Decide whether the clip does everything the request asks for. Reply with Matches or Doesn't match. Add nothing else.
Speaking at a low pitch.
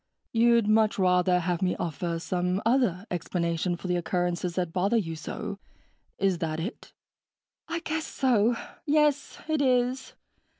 Doesn't match